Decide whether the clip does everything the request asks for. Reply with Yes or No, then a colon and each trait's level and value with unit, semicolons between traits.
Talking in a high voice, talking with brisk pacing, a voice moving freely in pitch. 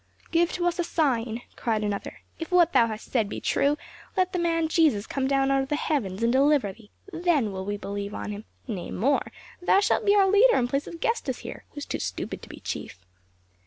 Yes: very high, 275 Hz; fast, 230 wpm; wide, 7.7 semitones